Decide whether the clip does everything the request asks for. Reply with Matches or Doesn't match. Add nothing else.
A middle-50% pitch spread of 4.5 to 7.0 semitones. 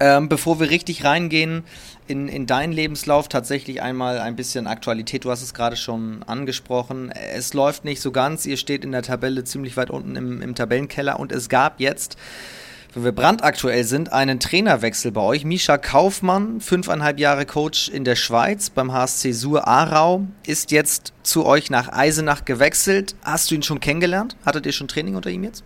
Doesn't match